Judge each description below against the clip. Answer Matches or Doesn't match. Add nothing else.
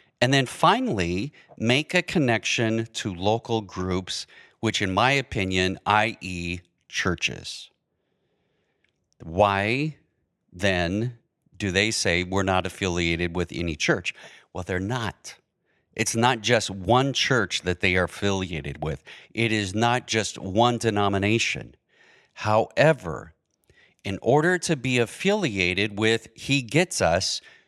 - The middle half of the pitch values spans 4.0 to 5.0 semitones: Matches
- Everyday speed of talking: Doesn't match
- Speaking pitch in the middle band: Doesn't match